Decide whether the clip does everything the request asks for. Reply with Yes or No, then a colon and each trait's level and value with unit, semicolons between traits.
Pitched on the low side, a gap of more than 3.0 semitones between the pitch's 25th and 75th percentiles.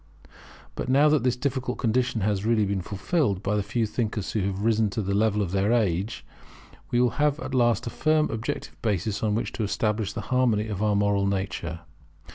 Yes: low, 110 Hz; average, 3.4 semitones